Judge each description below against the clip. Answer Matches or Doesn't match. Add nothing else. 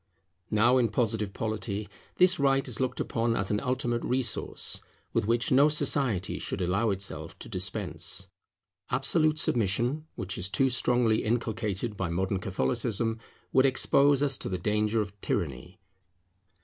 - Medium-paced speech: Matches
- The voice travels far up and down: Doesn't match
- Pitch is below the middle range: Matches